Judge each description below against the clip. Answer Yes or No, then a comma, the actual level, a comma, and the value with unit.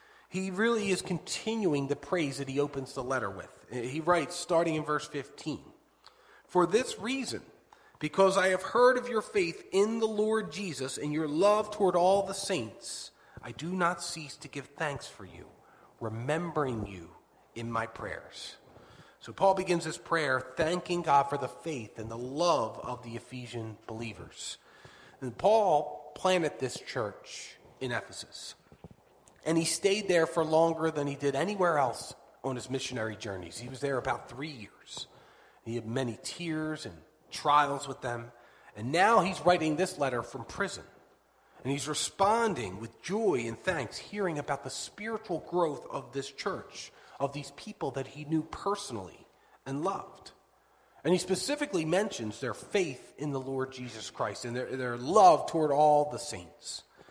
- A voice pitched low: No, medium, 150 Hz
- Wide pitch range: Yes, wide, 5.9 semitones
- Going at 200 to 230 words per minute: No, average, 165 wpm